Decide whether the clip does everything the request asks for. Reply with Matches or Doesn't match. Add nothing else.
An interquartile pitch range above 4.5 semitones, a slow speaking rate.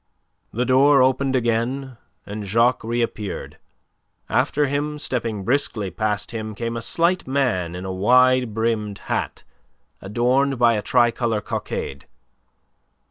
Doesn't match